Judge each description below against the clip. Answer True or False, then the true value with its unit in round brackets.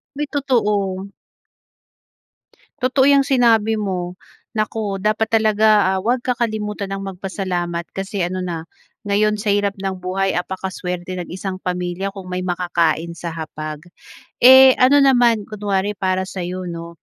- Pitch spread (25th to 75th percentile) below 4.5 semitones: True (3.2 semitones)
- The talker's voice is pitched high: True (195 Hz)